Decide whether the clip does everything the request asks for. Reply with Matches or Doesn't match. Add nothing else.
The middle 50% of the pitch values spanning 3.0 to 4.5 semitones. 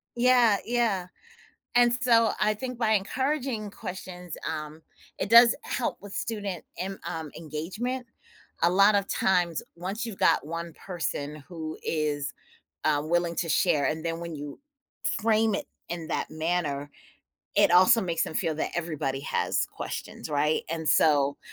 Doesn't match